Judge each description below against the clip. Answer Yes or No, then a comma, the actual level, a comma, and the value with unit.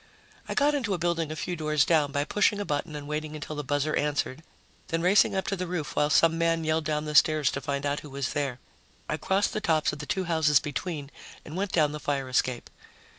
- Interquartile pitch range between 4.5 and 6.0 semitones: No, narrow, 2.6 semitones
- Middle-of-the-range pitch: Yes, medium, 155 Hz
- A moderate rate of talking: No, fast, 240 wpm